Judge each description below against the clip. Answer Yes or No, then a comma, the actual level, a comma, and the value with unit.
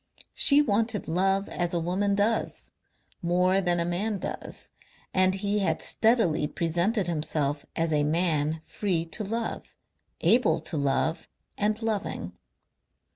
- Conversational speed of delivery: No, slow, 130 wpm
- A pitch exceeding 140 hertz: Yes, medium, 185 Hz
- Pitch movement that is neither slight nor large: Yes, average, 4.0 semitones